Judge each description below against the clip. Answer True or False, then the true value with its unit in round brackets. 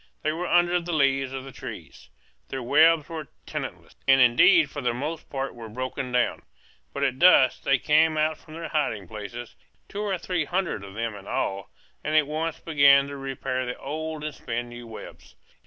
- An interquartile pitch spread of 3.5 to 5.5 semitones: True (4.2 semitones)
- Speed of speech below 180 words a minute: False (195 wpm)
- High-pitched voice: False (140 Hz)